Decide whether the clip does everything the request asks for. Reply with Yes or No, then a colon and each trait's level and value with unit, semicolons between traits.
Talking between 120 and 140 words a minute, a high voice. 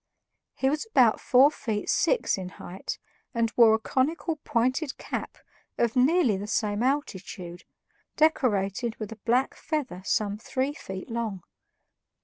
Yes: slow, 135 wpm; high, 235 Hz